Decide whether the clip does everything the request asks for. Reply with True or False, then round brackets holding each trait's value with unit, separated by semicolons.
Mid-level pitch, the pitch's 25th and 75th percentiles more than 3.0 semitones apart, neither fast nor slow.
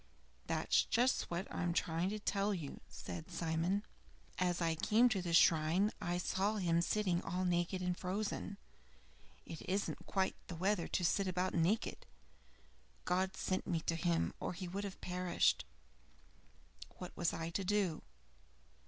False (180 Hz; 2.5 semitones; 155 wpm)